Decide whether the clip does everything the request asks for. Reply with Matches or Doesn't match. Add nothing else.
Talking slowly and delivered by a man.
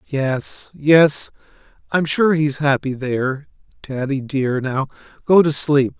Matches